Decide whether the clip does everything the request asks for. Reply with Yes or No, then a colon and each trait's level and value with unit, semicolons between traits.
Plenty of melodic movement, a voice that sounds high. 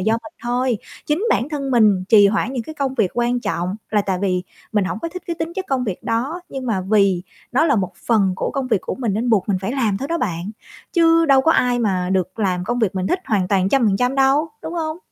Yes: wide, 5.7 semitones; high, 235 Hz